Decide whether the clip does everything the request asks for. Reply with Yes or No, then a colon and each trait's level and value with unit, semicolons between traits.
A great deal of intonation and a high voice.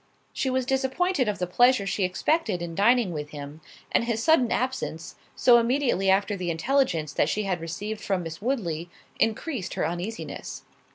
Yes: wide, 6.6 semitones; high, 210 Hz